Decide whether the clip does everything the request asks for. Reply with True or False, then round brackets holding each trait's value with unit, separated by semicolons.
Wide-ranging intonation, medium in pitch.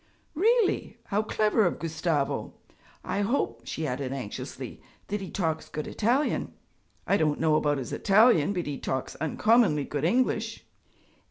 True (6.6 semitones; 170 Hz)